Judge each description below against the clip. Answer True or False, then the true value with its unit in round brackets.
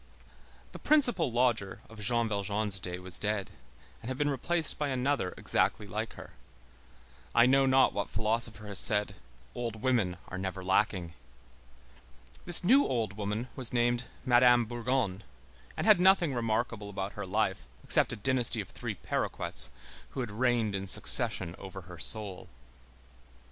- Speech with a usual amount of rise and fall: True (4.2 semitones)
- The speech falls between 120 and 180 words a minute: True (150 wpm)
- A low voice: True (115 Hz)